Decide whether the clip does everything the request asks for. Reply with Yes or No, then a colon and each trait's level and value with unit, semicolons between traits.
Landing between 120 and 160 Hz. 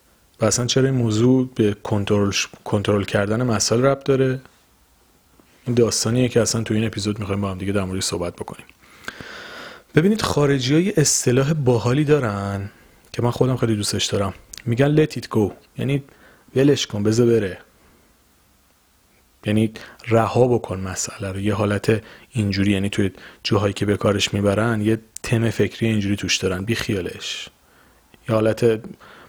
No: low, 110 Hz